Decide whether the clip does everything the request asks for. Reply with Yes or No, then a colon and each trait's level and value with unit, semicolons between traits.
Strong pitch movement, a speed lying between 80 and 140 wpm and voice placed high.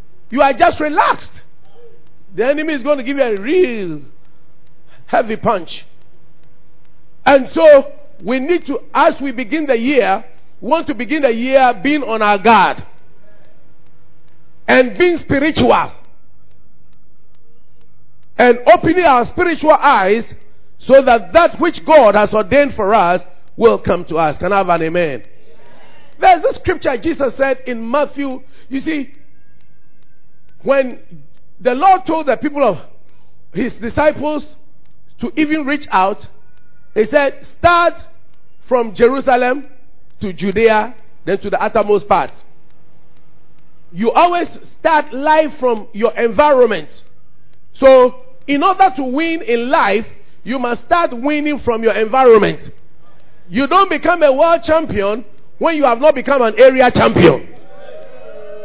Yes: wide, 5.9 semitones; slow, 135 wpm; very high, 260 Hz